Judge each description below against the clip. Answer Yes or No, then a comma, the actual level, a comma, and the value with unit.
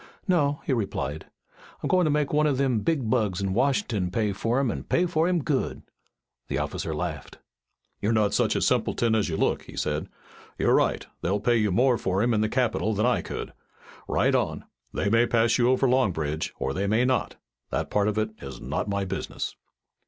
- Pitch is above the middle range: No, low, 110 Hz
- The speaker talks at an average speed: No, fast, 210 wpm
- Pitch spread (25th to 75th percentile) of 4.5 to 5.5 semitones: Yes, average, 4.8 semitones